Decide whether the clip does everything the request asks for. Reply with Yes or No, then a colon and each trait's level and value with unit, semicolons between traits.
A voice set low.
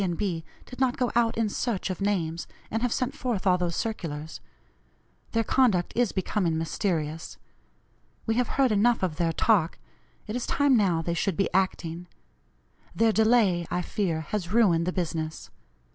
No: high, 190 Hz